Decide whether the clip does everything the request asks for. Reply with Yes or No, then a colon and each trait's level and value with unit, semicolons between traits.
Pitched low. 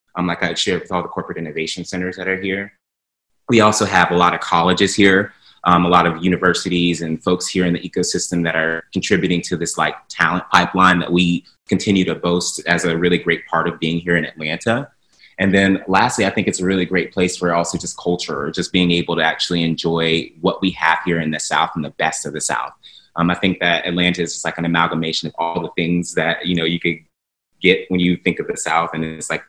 Yes: very low, 85 Hz